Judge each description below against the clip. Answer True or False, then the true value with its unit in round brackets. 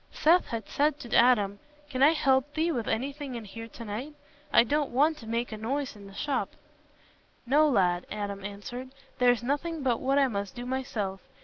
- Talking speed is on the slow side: False (195 wpm)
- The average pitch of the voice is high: True (245 Hz)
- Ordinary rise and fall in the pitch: True (4.8 semitones)